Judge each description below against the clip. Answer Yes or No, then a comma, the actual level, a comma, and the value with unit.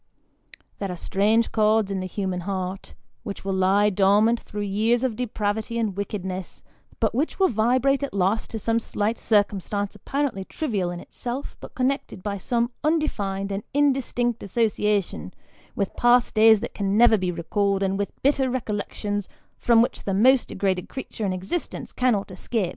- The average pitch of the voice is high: Yes, high, 210 Hz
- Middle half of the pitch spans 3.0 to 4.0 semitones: Yes, average, 3.5 semitones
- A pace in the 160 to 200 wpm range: Yes, average, 165 wpm